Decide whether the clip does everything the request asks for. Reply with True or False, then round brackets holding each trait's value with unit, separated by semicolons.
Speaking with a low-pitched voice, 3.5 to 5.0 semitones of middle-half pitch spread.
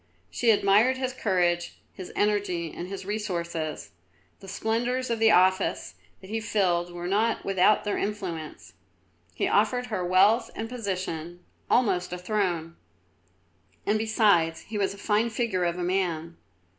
False (195 Hz; 3.8 semitones)